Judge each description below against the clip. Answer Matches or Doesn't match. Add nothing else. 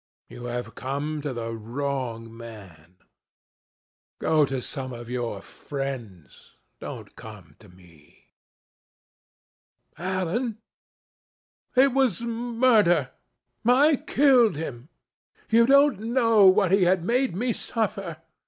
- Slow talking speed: Matches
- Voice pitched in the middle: Matches